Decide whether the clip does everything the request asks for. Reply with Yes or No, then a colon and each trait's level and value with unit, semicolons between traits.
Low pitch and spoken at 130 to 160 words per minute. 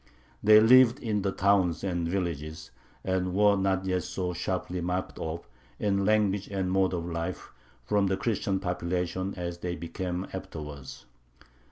Yes: very low, 95 Hz; average, 150 wpm